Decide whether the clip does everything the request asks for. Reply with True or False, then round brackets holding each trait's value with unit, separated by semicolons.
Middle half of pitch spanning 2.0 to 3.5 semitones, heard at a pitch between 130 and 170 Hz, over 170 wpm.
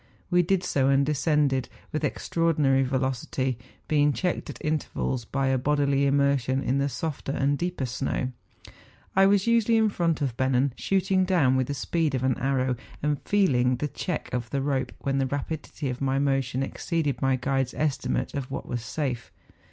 True (2.8 semitones; 140 Hz; 180 wpm)